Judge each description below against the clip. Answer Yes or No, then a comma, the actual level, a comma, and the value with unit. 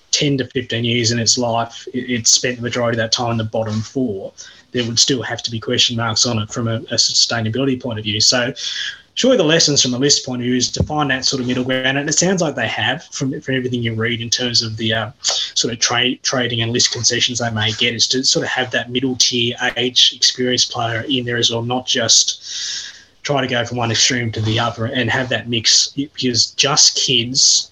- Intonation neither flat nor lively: No, narrow, 1.9 semitones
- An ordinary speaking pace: No, fast, 245 wpm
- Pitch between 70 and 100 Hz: No, low, 120 Hz